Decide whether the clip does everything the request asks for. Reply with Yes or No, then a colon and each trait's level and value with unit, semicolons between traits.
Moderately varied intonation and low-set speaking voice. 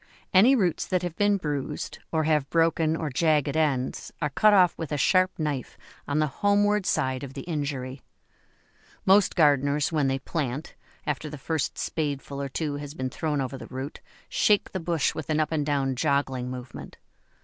No: average, 3.2 semitones; medium, 150 Hz